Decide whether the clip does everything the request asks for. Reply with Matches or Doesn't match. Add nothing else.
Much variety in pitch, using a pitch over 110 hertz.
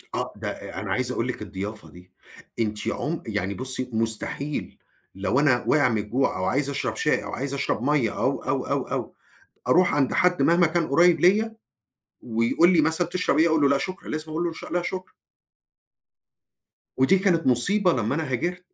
Matches